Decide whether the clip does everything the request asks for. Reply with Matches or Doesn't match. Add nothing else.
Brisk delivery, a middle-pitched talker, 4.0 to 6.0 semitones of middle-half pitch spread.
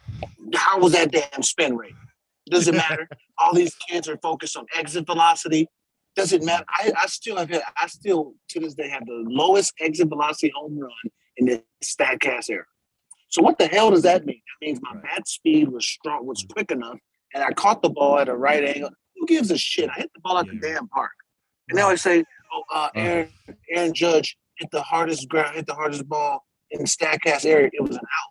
Doesn't match